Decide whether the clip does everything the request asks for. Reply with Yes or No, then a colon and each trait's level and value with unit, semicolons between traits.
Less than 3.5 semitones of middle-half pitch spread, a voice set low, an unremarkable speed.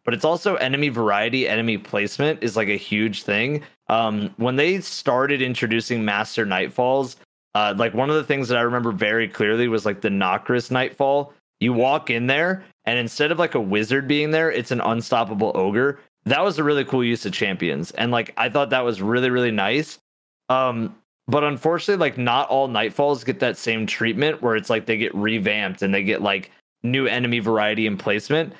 No: average, 4.2 semitones; low, 125 Hz; average, 195 wpm